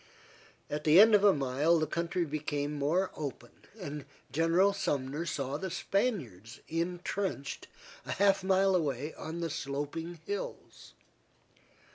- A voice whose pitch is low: No, medium, 165 Hz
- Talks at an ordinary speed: No, slow, 130 wpm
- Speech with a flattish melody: No, average, 4.6 semitones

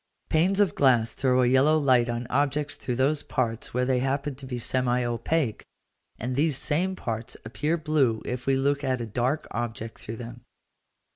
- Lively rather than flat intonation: No, average, 3.3 semitones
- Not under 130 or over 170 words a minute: No, average, 185 wpm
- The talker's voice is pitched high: No, low, 130 Hz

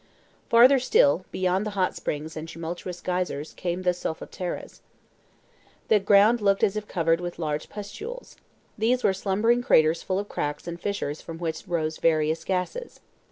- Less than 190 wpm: Yes, average, 160 wpm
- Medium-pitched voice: Yes, medium, 180 Hz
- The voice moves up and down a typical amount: Yes, average, 4.0 semitones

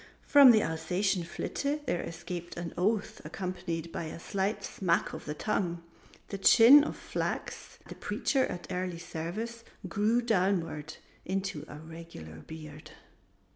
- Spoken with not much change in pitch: No, average, 4.2 semitones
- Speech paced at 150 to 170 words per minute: No, slow, 135 wpm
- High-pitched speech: No, medium, 180 Hz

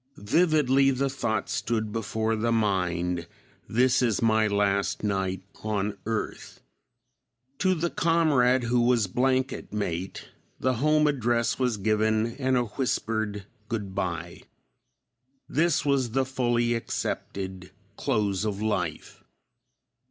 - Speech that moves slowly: Yes, slow, 115 wpm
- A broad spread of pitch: No, average, 4.1 semitones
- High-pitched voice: No, low, 115 Hz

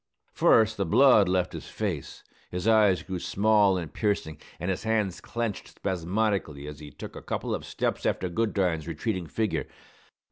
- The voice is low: Yes, very low, 95 Hz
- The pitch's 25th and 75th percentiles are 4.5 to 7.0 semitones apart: No, average, 3.9 semitones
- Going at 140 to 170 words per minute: Yes, average, 165 wpm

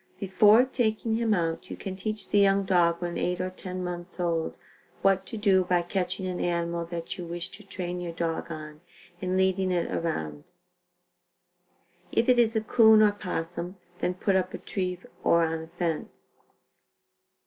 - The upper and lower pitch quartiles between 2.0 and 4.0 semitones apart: Yes, narrow, 2.6 semitones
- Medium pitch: Yes, medium, 180 Hz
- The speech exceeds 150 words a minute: Yes, average, 175 wpm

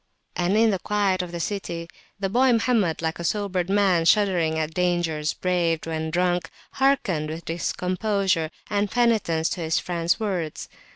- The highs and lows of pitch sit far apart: No, average, 3.6 semitones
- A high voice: No, medium, 180 Hz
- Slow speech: No, average, 160 wpm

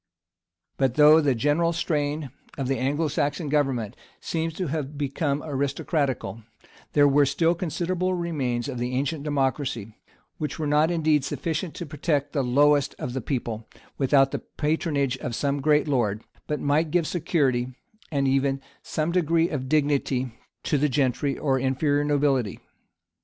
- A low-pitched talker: No, medium, 145 Hz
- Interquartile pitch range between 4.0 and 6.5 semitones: No, narrow, 2.6 semitones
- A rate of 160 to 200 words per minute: No, average, 150 wpm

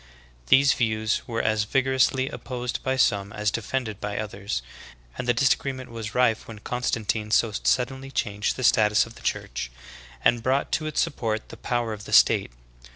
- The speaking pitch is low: Yes, low, 115 Hz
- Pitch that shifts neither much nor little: Yes, average, 3.4 semitones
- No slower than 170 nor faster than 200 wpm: Yes, average, 175 wpm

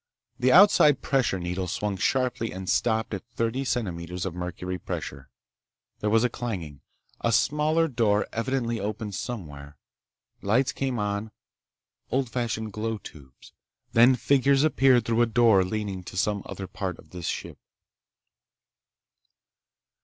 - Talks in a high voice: No, low, 110 Hz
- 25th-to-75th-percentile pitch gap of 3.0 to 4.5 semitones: No, average, 4.9 semitones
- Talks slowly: Yes, slow, 130 wpm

